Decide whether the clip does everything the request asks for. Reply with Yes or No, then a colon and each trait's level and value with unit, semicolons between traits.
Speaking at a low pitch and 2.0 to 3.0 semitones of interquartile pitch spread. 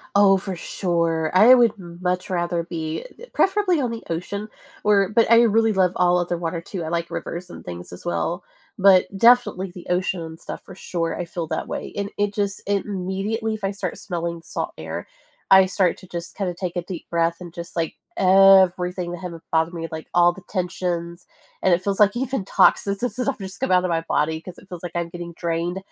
No: medium, 180 Hz; narrow, 2.6 semitones